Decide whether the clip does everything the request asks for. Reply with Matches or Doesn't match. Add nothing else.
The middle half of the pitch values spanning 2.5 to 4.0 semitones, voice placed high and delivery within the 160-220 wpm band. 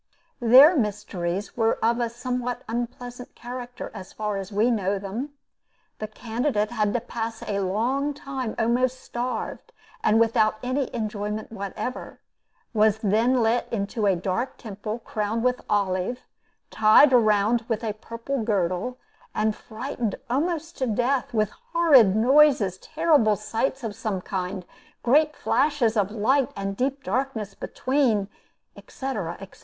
Doesn't match